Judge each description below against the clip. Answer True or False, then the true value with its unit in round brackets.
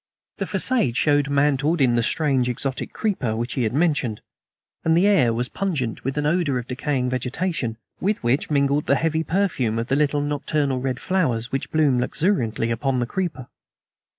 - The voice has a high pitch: False (140 Hz)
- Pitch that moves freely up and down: False (4.2 semitones)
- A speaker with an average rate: True (180 wpm)